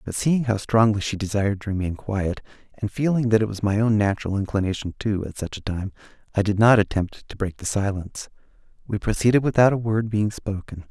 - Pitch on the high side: No, low, 105 Hz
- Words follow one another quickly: Yes, fast, 210 wpm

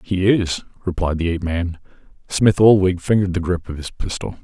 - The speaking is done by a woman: No, male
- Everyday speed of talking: Yes, average, 190 wpm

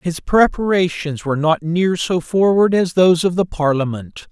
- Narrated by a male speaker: Yes, male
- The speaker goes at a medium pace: Yes, average, 165 wpm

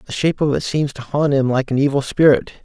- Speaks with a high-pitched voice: No, low, 135 Hz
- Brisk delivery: Yes, fast, 275 wpm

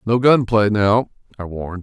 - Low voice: Yes, low, 105 Hz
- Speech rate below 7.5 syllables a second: Yes, 4.7 syllables/s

